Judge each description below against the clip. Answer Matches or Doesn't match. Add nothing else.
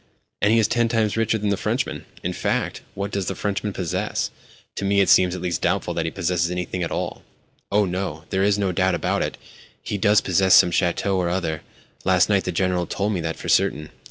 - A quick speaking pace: Matches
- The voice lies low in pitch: Matches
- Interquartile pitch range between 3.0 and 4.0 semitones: Doesn't match